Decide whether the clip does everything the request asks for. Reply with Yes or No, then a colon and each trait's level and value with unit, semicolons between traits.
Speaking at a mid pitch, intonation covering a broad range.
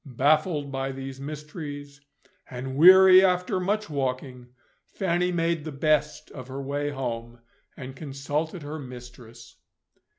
No: medium, 145 Hz; average, 3.5 semitones